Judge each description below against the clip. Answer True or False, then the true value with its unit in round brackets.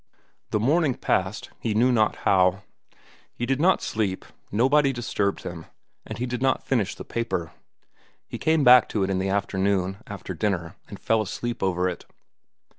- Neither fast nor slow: True (170 wpm)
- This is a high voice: False (105 Hz)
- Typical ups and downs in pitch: True (4.6 semitones)